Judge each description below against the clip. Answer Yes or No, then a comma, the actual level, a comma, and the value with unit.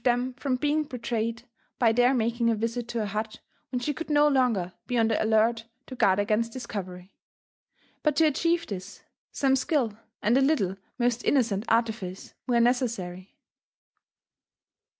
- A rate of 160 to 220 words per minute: Yes, average, 165 wpm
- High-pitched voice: Yes, high, 235 Hz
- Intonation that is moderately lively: Yes, average, 3.1 semitones